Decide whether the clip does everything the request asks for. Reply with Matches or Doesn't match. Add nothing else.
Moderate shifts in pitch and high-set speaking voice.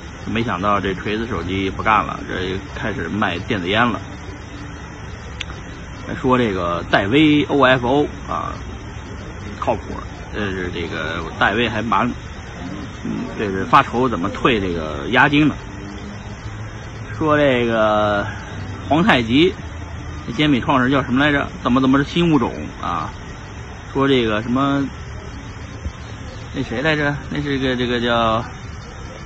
Doesn't match